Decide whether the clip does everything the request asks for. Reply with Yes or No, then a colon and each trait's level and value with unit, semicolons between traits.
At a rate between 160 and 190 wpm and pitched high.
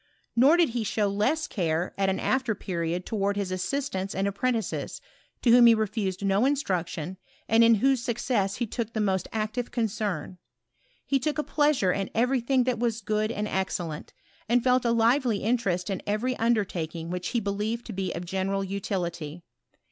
Yes: average, 180 wpm; high, 215 Hz